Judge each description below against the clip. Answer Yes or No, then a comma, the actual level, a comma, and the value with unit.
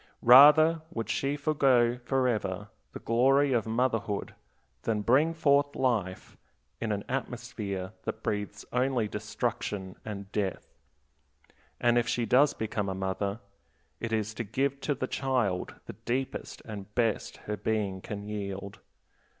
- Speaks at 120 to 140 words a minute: Yes, slow, 135 wpm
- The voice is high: No, low, 115 Hz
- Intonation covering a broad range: No, average, 4.2 semitones